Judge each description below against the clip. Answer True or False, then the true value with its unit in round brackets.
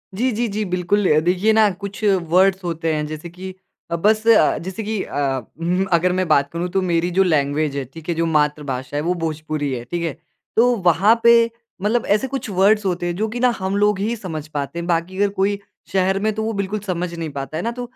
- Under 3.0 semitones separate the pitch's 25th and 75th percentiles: False (4.6 semitones)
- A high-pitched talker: False (180 Hz)